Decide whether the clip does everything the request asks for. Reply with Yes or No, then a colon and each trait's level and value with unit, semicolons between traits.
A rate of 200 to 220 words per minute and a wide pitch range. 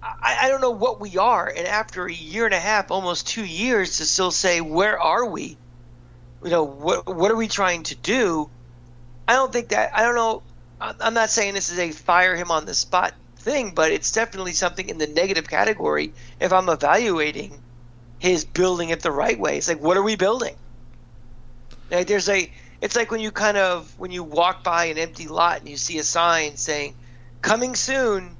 Yes: fast, 205 wpm; wide, 5.9 semitones